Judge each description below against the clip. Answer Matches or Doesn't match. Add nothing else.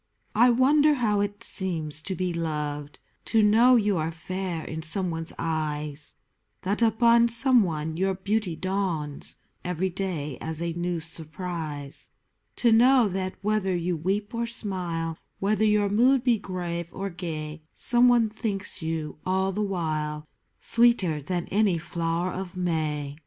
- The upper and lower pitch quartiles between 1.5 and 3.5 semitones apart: Doesn't match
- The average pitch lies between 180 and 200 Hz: Matches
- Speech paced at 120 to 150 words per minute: Matches